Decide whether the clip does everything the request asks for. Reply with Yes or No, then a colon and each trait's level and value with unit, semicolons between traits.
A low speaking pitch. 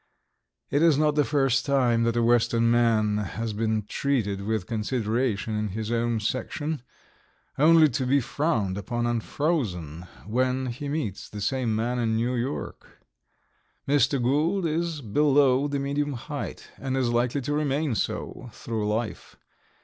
Yes: low, 125 Hz